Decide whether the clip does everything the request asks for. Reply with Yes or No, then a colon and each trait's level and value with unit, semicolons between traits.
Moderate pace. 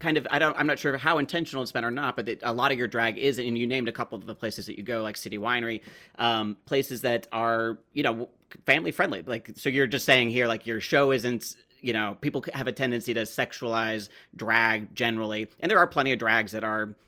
No: fast, 250 wpm